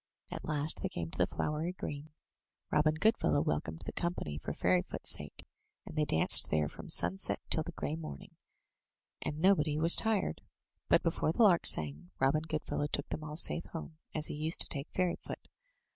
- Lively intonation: Yes, wide, 8.6 semitones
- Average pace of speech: Yes, average, 180 wpm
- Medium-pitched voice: Yes, medium, 150 Hz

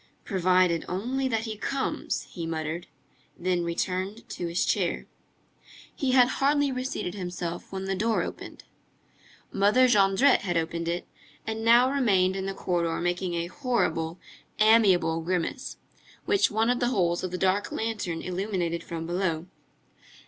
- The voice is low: No, high, 190 Hz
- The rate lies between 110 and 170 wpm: Yes, average, 150 wpm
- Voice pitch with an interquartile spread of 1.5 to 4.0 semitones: No, average, 4.6 semitones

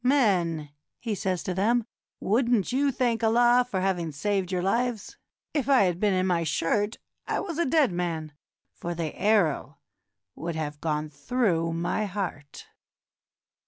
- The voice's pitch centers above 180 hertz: Yes, high, 190 Hz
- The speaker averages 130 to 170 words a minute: Yes, average, 160 wpm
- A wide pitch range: Yes, wide, 6.0 semitones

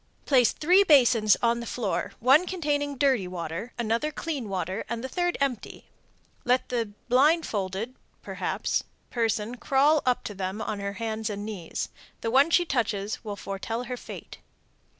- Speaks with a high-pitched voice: Yes, high, 235 Hz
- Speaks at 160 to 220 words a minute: No, average, 150 wpm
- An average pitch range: Yes, average, 4.9 semitones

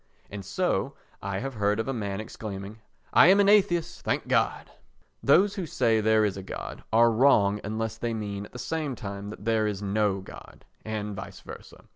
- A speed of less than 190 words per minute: No, average, 195 wpm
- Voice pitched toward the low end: Yes, low, 110 Hz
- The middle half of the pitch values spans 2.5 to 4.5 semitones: Yes, average, 3.5 semitones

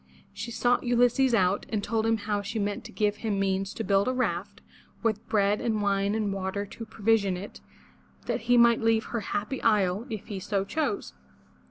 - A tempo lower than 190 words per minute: No, average, 195 wpm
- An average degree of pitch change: No, narrow, 2.3 semitones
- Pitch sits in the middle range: No, high, 210 Hz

